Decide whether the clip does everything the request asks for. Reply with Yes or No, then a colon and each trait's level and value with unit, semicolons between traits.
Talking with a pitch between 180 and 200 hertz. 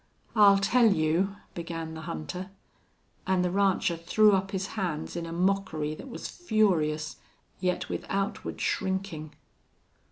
Yes: medium, 185 Hz